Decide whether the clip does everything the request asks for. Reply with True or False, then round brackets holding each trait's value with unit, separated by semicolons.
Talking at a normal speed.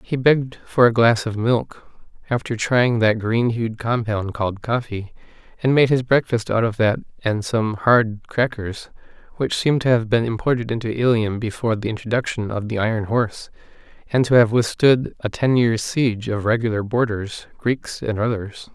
True (175 wpm)